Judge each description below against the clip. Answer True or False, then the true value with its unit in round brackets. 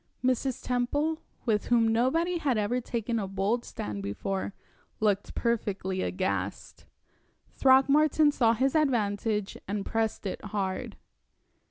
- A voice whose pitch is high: True (225 Hz)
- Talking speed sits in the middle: False (120 wpm)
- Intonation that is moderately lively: True (4.6 semitones)